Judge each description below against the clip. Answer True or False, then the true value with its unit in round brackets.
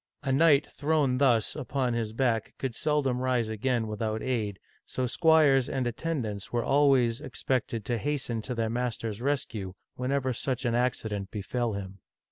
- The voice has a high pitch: False (125 Hz)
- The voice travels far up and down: False (3.2 semitones)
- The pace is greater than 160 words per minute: False (155 wpm)